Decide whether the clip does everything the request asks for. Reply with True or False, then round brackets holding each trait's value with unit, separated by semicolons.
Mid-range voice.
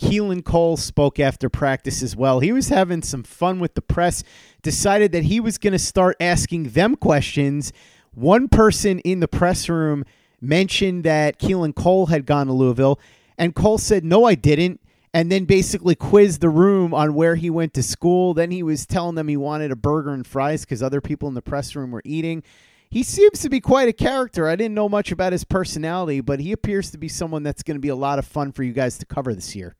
True (160 Hz)